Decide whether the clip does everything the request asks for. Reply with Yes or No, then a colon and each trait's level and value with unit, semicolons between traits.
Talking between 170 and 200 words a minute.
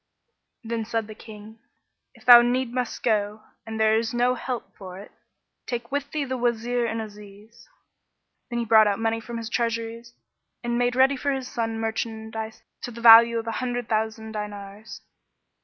Yes: average, 180 wpm